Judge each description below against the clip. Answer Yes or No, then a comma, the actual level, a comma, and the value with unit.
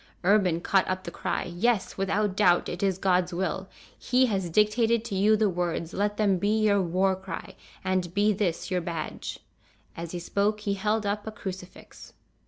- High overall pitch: Yes, high, 195 Hz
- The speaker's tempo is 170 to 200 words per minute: Yes, average, 185 wpm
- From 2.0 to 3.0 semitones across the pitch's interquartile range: Yes, average, 2.7 semitones